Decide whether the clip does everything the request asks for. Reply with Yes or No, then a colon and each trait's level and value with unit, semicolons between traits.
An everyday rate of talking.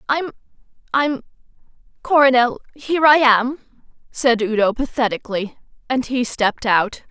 No: slow, 95 wpm